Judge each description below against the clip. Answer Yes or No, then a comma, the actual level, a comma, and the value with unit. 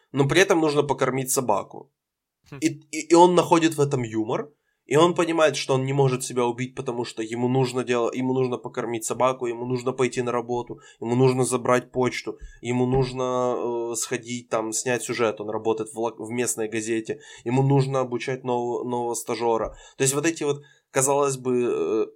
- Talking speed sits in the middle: No, fast, 185 wpm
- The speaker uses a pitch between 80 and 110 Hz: No, low, 125 Hz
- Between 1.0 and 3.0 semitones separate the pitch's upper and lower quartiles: Yes, narrow, 2.4 semitones